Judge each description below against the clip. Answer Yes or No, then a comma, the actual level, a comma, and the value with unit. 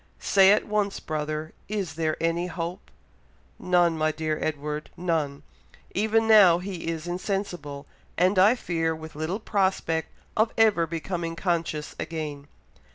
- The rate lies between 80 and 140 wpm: Yes, slow, 135 wpm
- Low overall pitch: No, medium, 170 Hz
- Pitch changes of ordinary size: Yes, average, 3.6 semitones